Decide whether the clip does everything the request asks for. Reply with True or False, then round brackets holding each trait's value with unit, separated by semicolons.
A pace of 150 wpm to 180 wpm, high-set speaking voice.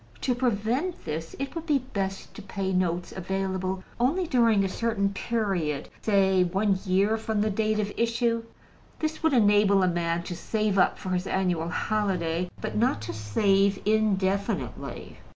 True (160 wpm; 200 Hz)